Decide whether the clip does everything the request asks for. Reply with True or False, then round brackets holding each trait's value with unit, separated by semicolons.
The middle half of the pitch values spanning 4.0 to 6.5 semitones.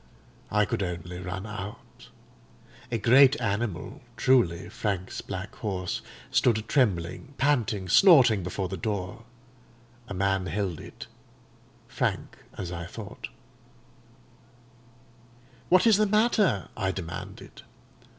True (5.1 semitones)